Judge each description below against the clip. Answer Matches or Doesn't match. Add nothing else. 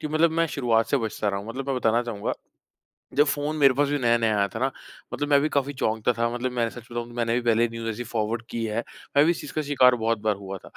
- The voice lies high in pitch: Doesn't match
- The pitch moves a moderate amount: Matches